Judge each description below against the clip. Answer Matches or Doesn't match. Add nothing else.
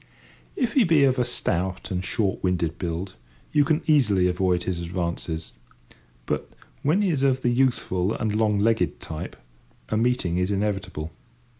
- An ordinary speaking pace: Matches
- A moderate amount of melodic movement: Doesn't match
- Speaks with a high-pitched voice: Doesn't match